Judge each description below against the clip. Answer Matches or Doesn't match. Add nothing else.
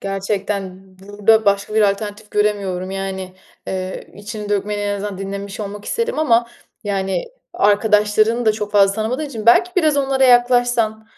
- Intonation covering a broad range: Doesn't match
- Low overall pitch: Doesn't match